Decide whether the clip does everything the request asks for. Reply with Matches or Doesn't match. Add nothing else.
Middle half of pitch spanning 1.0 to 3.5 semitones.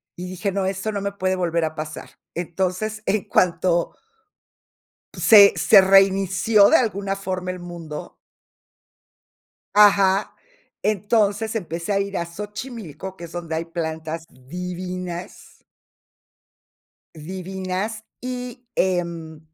Matches